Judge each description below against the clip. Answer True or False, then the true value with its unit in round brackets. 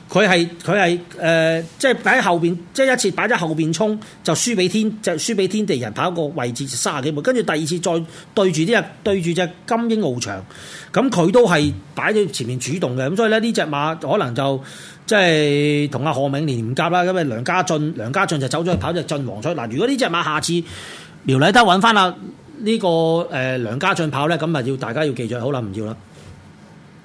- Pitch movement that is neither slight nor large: True (4.9 semitones)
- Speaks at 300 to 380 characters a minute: True (305 characters per minute)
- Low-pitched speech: False (170 Hz)